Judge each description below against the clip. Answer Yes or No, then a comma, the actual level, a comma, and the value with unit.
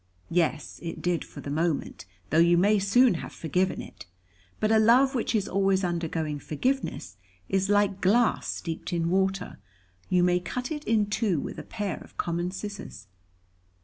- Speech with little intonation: No, average, 3.8 semitones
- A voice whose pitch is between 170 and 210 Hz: Yes, high, 190 Hz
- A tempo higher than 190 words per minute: No, average, 170 wpm